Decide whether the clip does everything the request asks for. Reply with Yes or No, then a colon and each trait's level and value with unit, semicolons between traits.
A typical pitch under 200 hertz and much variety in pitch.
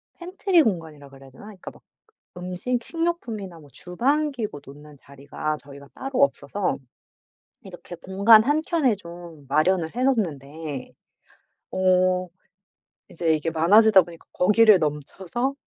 Yes: medium, 185 Hz; wide, 6.8 semitones